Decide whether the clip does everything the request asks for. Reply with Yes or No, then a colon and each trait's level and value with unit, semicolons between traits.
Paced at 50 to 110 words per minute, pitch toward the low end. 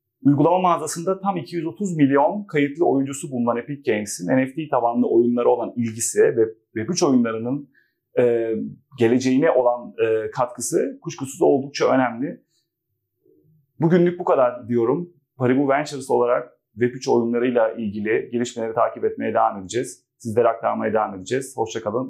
No: average, 125 wpm; low, 130 Hz